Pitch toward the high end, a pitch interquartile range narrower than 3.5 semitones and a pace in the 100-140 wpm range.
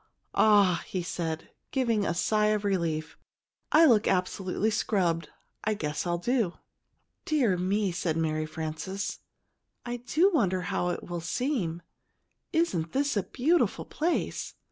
No: high, 195 Hz; wide, 5.5 semitones; slow, 135 wpm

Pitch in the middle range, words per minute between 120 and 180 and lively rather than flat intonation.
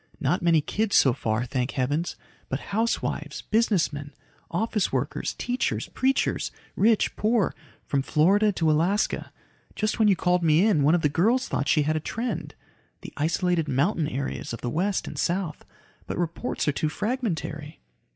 Yes: medium, 170 Hz; average, 160 wpm; wide, 6.0 semitones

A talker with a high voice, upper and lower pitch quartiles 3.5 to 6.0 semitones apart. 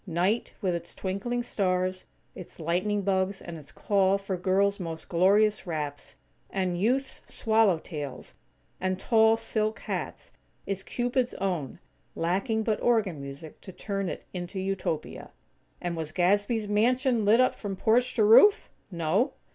Yes: high, 195 Hz; average, 3.9 semitones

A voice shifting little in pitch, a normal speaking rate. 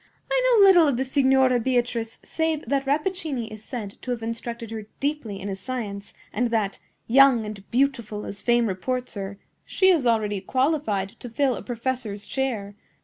No: average, 4.2 semitones; average, 175 wpm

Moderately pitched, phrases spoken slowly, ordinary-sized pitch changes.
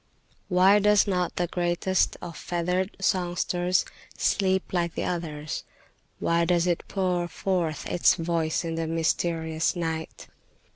No: medium, 175 Hz; slow, 130 wpm; narrow, 1.8 semitones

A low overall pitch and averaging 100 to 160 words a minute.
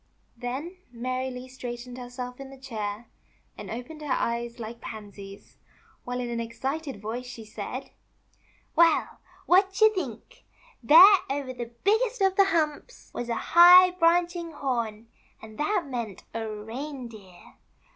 No: very high, 255 Hz; average, 145 wpm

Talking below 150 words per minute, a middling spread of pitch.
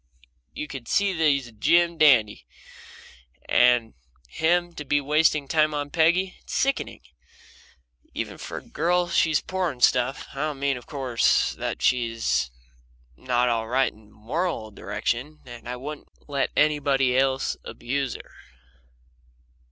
Yes: average, 140 wpm; average, 4.2 semitones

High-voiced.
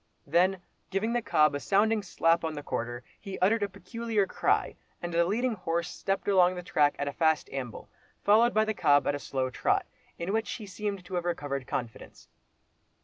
No: medium, 180 Hz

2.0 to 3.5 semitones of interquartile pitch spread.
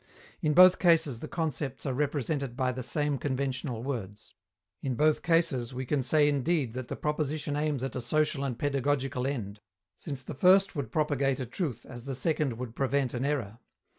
Yes: average, 3.1 semitones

